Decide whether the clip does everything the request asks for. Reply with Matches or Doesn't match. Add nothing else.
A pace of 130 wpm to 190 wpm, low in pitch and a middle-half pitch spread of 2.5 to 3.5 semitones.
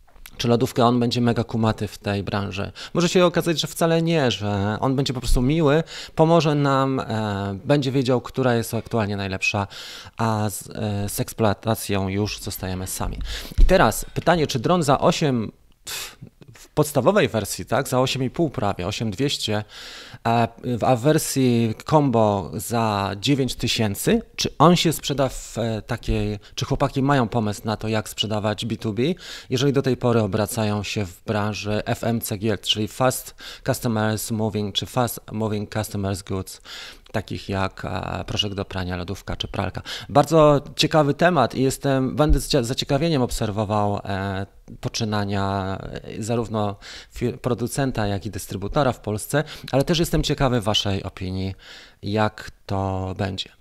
Doesn't match